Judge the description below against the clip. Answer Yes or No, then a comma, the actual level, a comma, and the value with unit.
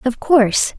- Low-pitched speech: No, very high, 250 Hz